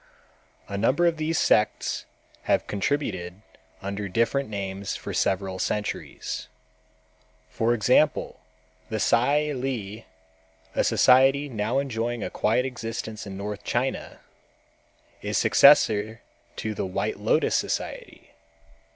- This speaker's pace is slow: Yes, slow, 110 wpm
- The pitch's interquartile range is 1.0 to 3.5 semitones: No, average, 4.8 semitones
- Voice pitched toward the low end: Yes, low, 110 Hz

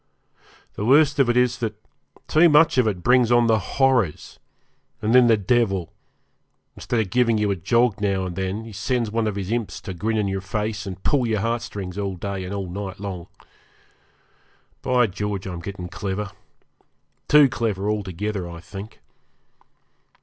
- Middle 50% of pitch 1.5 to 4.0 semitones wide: Yes, average, 3.7 semitones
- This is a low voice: Yes, low, 105 Hz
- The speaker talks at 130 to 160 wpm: No, average, 170 wpm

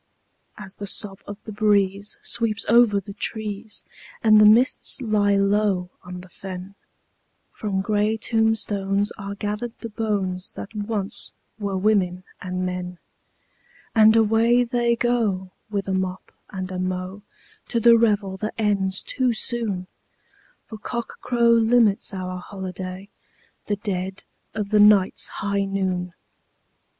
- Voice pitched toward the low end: No, high, 205 Hz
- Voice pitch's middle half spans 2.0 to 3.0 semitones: Yes, narrow, 2.6 semitones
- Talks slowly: Yes, slow, 130 wpm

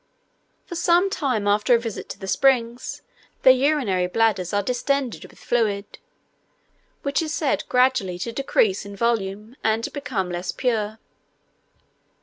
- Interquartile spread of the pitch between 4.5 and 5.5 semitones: Yes, average, 5.0 semitones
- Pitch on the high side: Yes, high, 235 Hz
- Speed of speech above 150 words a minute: No, average, 140 wpm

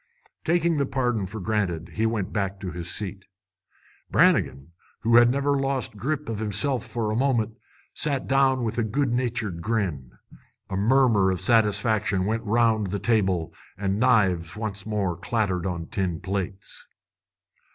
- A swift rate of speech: No, average, 155 wpm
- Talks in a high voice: No, low, 110 Hz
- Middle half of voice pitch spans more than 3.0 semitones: Yes, average, 4.2 semitones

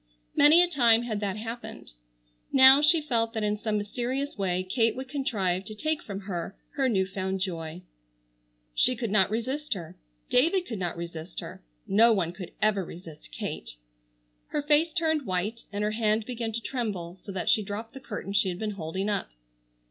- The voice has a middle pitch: No, high, 215 Hz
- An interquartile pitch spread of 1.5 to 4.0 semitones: No, average, 5.2 semitones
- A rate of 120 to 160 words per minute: No, average, 180 wpm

